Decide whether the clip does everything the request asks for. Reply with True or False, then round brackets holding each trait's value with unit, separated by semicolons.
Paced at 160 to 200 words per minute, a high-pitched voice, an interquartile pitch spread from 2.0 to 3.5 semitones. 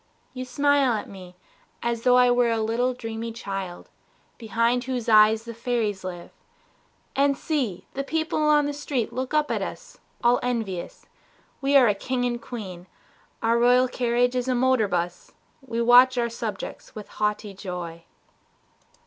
True (165 wpm; 235 Hz; 3.1 semitones)